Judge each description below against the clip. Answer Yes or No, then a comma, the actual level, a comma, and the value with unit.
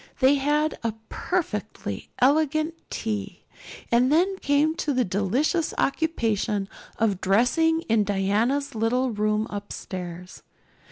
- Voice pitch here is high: Yes, high, 235 Hz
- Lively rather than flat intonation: Yes, wide, 6.5 semitones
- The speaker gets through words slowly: Yes, slow, 105 wpm